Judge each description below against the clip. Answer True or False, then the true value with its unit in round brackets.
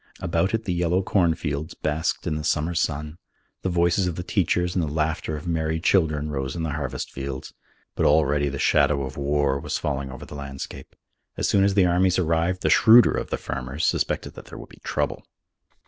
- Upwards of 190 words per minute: True (205 wpm)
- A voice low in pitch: True (80 Hz)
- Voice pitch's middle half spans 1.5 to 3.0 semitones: False (3.5 semitones)